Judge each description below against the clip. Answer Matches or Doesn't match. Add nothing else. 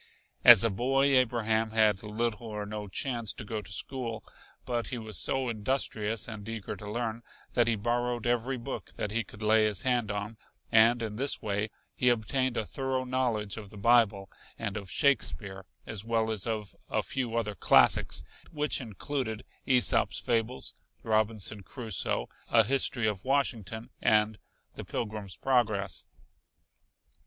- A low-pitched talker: Matches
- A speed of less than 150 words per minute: Doesn't match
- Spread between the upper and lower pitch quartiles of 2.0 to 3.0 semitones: Matches